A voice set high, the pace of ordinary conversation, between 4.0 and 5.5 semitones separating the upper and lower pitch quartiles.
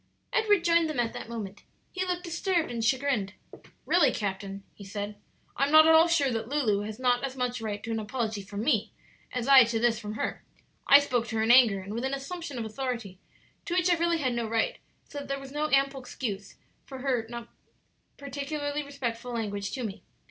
No: very high, 250 Hz; fast, 215 wpm; average, 4.6 semitones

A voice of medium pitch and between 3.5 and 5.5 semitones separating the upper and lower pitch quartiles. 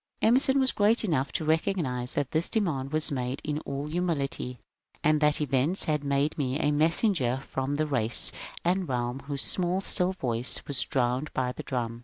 Yes: medium, 145 Hz; average, 4.5 semitones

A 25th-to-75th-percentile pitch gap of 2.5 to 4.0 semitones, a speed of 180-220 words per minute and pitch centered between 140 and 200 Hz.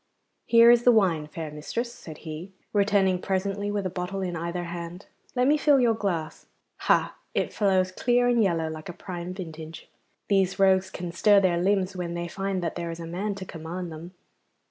Yes: average, 3.0 semitones; average, 195 wpm; medium, 185 Hz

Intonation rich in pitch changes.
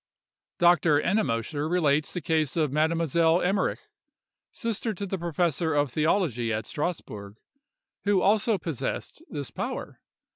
No: average, 3.8 semitones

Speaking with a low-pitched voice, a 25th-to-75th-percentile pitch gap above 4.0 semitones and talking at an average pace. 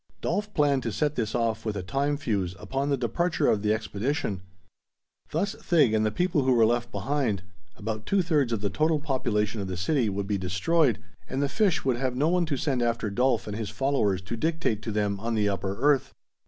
No: low, 120 Hz; wide, 5.6 semitones; fast, 220 wpm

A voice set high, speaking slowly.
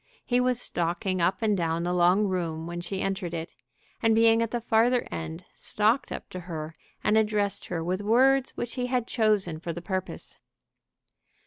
No: high, 195 Hz; average, 185 wpm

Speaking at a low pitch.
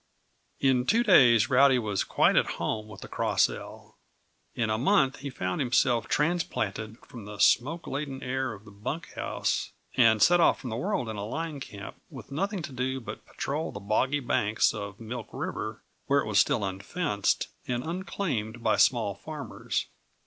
Yes: low, 125 Hz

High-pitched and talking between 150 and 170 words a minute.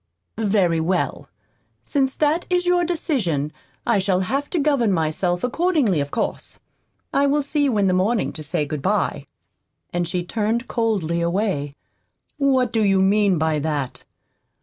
Yes: high, 205 Hz; average, 155 wpm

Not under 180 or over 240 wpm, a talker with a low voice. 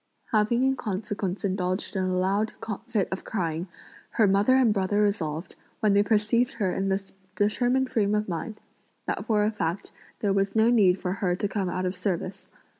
No: average, 190 wpm; high, 200 Hz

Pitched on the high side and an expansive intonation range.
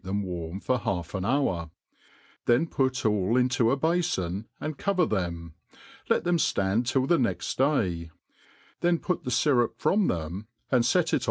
No: low, 120 Hz; wide, 7.3 semitones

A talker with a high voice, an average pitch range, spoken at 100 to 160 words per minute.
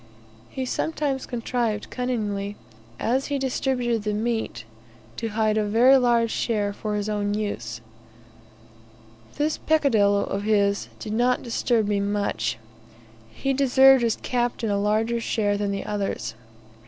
Yes: high, 220 Hz; average, 3.4 semitones; slow, 135 wpm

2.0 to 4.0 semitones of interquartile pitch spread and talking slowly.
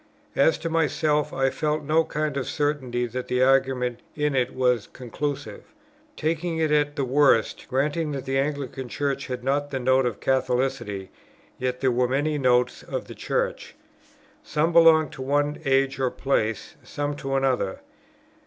No: average, 2.7 semitones; average, 165 wpm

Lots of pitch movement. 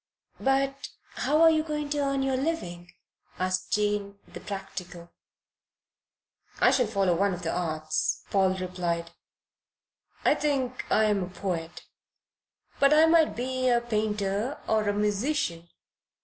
Yes: wide, 6.8 semitones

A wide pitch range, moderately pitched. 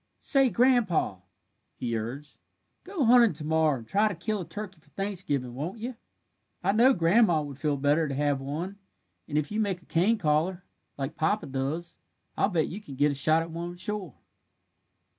Yes: wide, 6.1 semitones; medium, 165 Hz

